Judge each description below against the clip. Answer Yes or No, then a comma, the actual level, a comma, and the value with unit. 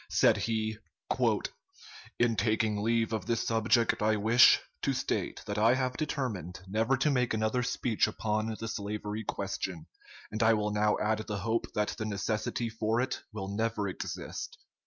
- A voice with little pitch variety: Yes, narrow, 1.7 semitones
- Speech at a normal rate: Yes, average, 160 wpm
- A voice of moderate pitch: No, low, 110 Hz